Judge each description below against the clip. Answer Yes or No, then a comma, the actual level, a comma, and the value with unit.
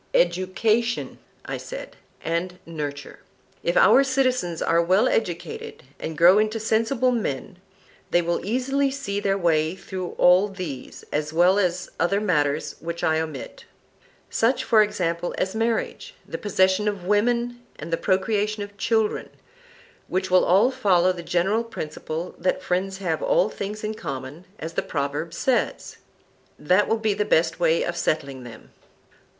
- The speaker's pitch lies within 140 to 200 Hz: Yes, high, 190 Hz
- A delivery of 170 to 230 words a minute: No, average, 150 wpm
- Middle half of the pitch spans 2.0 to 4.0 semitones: No, average, 4.8 semitones